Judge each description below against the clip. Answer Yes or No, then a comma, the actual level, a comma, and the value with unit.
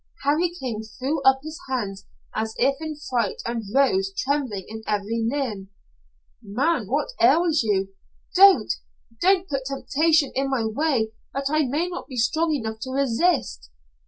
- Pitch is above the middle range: Yes, very high, 265 Hz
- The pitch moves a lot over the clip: Yes, wide, 5.7 semitones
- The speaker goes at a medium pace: Yes, average, 155 wpm